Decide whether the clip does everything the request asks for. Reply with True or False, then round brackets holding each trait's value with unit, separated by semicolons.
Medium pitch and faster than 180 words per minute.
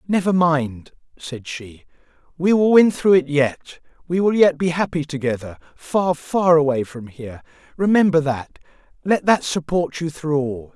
False (155 Hz; 145 wpm)